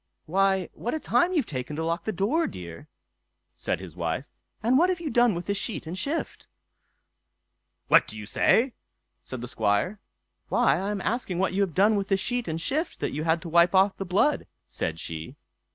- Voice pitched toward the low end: No, high, 190 Hz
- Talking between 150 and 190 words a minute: No, fast, 205 wpm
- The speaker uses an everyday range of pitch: No, wide, 7.2 semitones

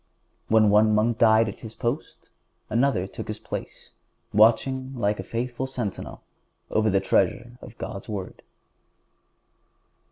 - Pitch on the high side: No, low, 110 Hz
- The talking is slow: Yes, slow, 130 wpm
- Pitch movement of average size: No, narrow, 2.3 semitones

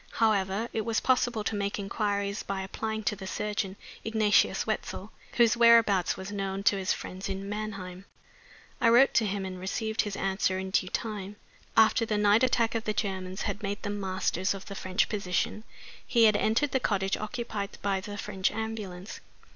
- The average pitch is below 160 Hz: No, high, 205 Hz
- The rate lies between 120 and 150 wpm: No, average, 180 wpm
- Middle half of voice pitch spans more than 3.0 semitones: No, narrow, 2.4 semitones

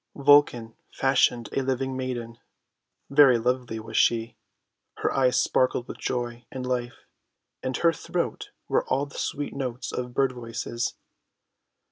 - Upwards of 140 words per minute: No, slow, 135 wpm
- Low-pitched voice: Yes, low, 125 Hz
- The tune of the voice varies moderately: No, narrow, 2.0 semitones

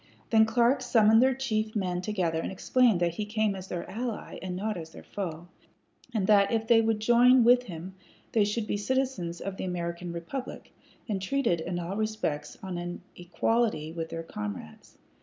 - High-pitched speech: Yes, high, 205 Hz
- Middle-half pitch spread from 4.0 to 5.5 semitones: Yes, average, 4.5 semitones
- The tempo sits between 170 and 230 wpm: Yes, average, 185 wpm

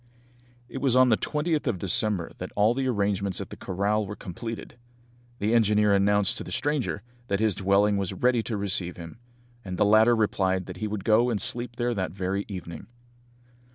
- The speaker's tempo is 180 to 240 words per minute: Yes, average, 190 wpm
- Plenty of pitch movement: No, average, 3.1 semitones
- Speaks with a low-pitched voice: Yes, low, 105 Hz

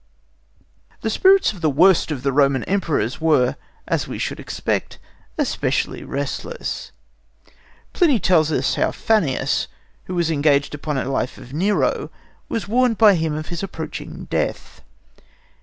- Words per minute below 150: Yes, average, 140 wpm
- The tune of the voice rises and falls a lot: Yes, wide, 5.8 semitones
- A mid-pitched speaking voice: Yes, medium, 160 Hz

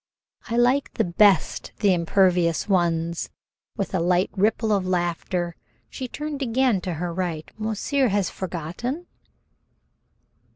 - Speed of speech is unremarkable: No, slow, 120 wpm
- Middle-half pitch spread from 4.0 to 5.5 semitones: Yes, average, 4.5 semitones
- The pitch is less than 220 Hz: Yes, high, 190 Hz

